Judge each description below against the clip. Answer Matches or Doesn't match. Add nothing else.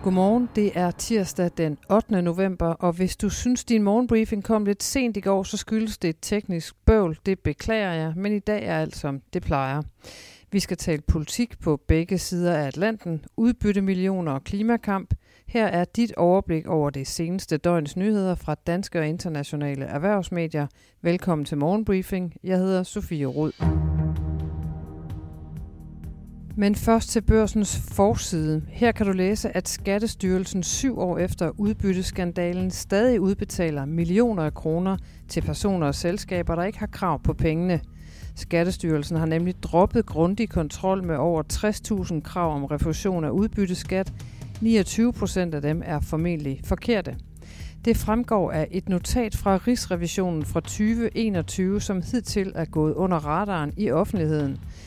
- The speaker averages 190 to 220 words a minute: Doesn't match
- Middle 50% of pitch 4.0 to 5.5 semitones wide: Matches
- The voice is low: Doesn't match